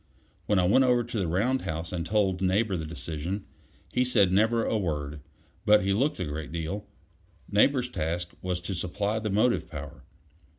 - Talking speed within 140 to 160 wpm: No, average, 180 wpm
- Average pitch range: Yes, average, 4.5 semitones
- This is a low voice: Yes, very low, 95 Hz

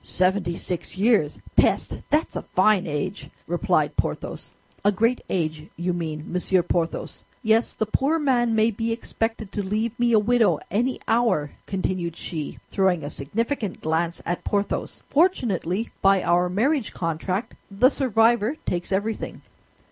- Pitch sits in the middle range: No, high, 200 Hz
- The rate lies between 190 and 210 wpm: No, average, 145 wpm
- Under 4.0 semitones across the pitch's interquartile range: No, average, 4.7 semitones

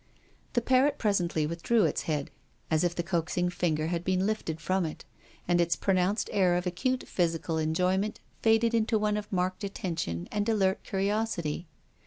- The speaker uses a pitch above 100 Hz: Yes, medium, 185 Hz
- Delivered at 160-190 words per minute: Yes, average, 165 wpm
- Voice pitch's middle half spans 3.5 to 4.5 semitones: Yes, average, 3.8 semitones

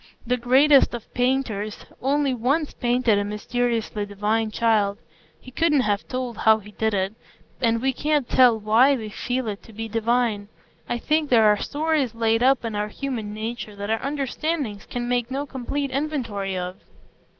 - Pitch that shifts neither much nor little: Yes, average, 3.8 semitones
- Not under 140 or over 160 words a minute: No, average, 170 wpm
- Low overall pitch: No, high, 235 Hz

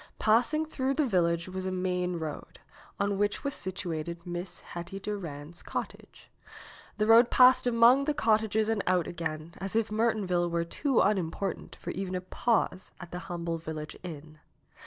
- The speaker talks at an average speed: Yes, average, 160 wpm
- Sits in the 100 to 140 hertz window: No, medium, 185 Hz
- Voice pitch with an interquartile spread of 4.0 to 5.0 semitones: Yes, average, 4.4 semitones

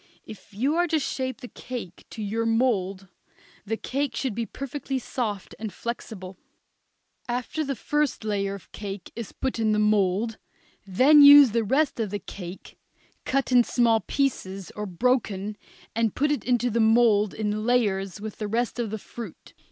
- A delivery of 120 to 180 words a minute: Yes, average, 165 wpm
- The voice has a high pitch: Yes, high, 225 Hz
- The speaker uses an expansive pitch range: No, average, 3.7 semitones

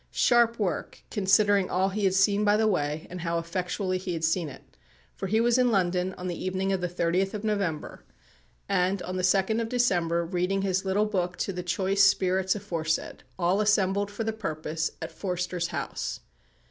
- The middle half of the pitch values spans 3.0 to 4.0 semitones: No, narrow, 2.4 semitones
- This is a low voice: No, high, 190 Hz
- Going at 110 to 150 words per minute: No, average, 190 wpm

